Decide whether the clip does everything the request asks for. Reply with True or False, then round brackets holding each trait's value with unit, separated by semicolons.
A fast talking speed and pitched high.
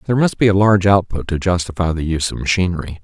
False (235 wpm; 90 Hz)